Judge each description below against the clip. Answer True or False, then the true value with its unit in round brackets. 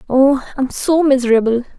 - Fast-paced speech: False (135 wpm)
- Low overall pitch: False (265 Hz)